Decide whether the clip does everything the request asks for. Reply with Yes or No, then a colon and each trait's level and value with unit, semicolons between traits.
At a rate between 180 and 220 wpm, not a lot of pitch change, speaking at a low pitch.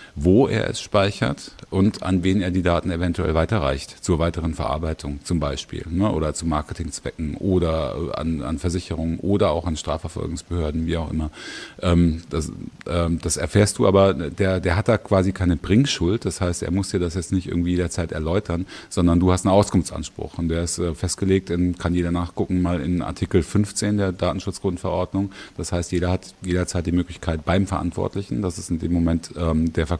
Yes: average, 185 wpm; narrow, 2.3 semitones; very low, 90 Hz